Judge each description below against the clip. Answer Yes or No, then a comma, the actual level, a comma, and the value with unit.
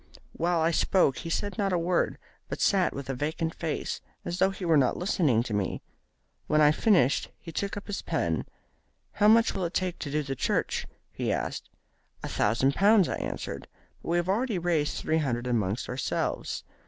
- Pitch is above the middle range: No, medium, 165 Hz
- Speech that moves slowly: No, average, 200 wpm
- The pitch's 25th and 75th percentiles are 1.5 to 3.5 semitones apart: No, average, 5.3 semitones